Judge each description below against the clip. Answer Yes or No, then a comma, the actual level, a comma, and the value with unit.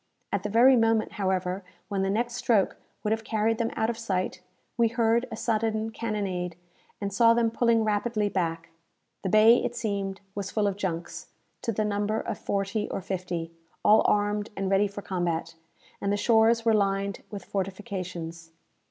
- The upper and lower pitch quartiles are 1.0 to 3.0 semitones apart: Yes, narrow, 2.6 semitones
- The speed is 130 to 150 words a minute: No, average, 175 wpm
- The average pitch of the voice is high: Yes, high, 205 Hz